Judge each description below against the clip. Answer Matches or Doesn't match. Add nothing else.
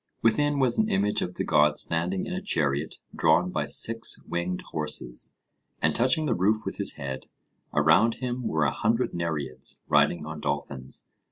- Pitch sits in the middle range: Doesn't match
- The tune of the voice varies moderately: Doesn't match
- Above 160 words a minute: Matches